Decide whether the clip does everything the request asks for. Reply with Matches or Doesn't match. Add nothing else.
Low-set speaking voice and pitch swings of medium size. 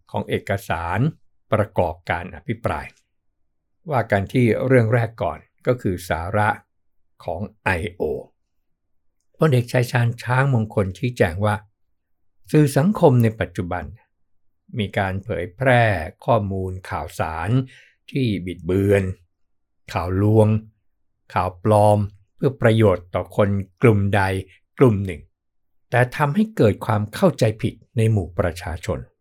Matches